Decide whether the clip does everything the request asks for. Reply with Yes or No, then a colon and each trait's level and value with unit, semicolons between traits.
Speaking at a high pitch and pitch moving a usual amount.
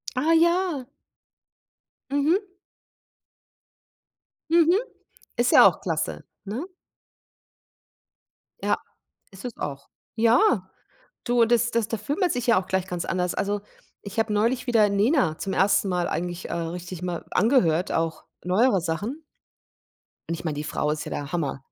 No: high, 205 Hz; wide, 6.0 semitones